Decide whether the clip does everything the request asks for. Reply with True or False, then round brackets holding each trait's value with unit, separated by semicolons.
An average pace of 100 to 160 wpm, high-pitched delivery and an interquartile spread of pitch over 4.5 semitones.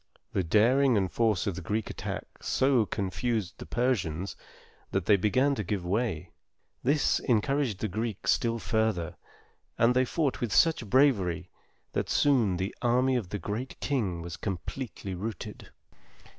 False (150 wpm; 110 Hz; 5.0 semitones)